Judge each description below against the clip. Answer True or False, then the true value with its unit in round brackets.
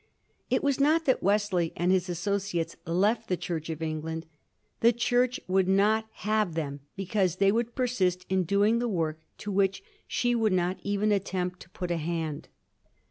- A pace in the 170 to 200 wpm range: True (180 wpm)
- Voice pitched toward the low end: False (190 Hz)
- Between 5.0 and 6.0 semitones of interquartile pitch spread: False (3.8 semitones)